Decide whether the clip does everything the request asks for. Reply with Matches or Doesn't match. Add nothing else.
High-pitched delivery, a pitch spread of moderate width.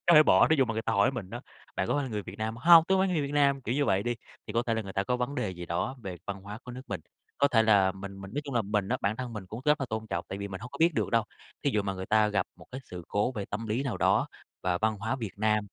Doesn't match